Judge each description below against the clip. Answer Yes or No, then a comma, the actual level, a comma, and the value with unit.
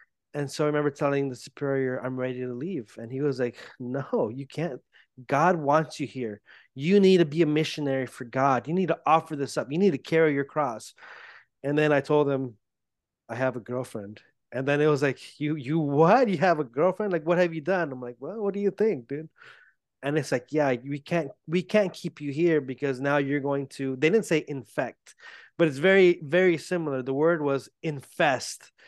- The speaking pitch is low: No, medium, 145 Hz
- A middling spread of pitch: Yes, average, 3.7 semitones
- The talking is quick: Yes, fast, 220 wpm